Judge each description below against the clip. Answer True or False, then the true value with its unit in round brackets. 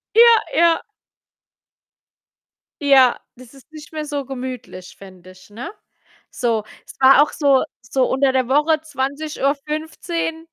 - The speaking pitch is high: True (275 Hz)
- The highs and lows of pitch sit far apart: False (3.4 semitones)